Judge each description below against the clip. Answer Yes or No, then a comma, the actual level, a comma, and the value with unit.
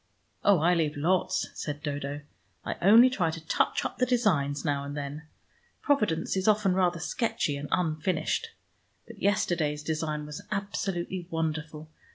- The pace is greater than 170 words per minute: No, average, 150 wpm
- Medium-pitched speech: Yes, medium, 160 Hz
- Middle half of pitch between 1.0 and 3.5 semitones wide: No, average, 4.2 semitones